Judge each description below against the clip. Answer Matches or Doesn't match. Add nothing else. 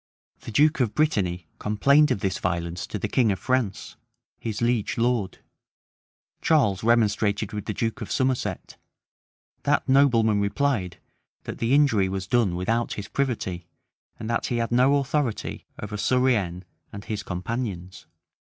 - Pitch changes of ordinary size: Matches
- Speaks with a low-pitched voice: Matches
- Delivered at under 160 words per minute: Matches